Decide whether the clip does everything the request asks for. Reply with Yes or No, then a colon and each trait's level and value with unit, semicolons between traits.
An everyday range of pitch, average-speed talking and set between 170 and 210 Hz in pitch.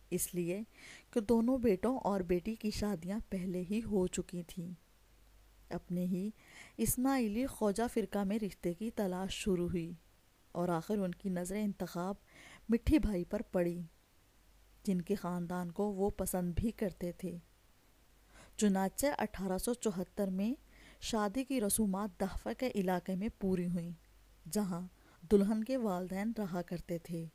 Yes: average, 3.3 semitones; average, 145 wpm; high, 190 Hz